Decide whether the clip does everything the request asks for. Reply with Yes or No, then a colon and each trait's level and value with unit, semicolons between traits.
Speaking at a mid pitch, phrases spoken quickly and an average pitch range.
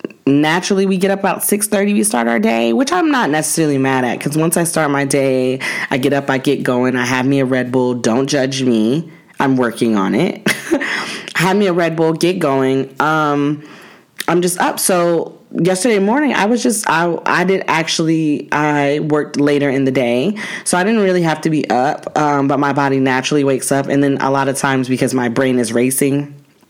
Yes: medium, 145 Hz; fast, 215 wpm; average, 4.6 semitones